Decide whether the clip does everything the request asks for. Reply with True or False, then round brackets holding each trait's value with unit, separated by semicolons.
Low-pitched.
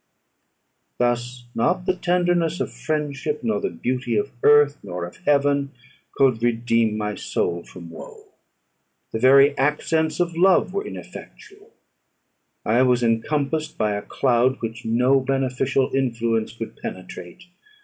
True (130 Hz)